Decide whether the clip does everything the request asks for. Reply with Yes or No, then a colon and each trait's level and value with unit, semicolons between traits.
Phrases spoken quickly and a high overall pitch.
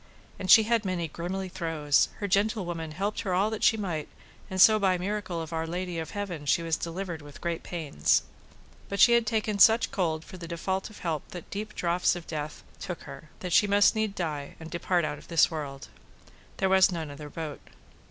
No: fast, 210 wpm; medium, 175 Hz